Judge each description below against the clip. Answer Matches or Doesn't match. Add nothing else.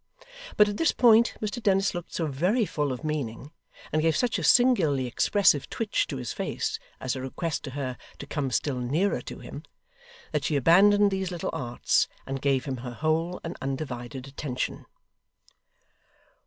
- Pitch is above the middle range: Doesn't match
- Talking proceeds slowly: Doesn't match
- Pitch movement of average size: Doesn't match